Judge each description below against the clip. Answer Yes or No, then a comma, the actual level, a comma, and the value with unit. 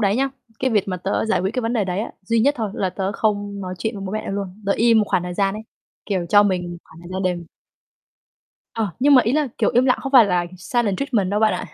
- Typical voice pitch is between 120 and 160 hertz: No, high, 205 Hz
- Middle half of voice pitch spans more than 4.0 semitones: No, average, 3.4 semitones